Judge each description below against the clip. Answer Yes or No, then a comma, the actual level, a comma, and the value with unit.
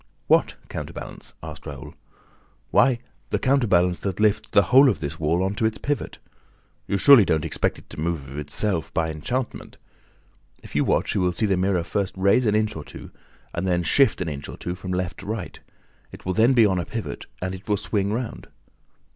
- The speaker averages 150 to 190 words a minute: No, fast, 205 wpm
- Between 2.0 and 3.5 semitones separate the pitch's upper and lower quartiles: No, average, 3.9 semitones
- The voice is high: No, very low, 95 Hz